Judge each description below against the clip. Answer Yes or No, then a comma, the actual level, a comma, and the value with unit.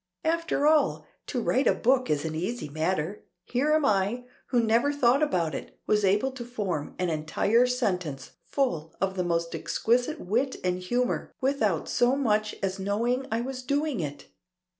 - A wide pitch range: Yes, wide, 6.2 semitones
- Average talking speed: Yes, average, 170 wpm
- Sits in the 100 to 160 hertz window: No, high, 230 Hz